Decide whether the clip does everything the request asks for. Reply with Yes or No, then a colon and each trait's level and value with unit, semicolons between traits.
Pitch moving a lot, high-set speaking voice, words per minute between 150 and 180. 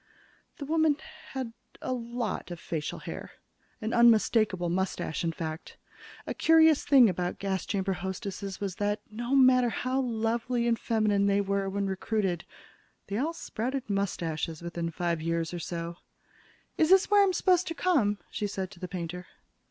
Yes: wide, 5.8 semitones; high, 205 Hz; average, 160 wpm